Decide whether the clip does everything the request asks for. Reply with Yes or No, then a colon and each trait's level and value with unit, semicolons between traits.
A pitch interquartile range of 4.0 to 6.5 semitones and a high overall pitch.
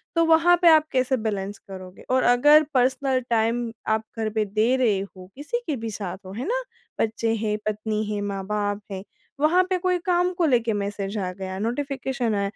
Yes: average, 5.2 semitones; high, 225 Hz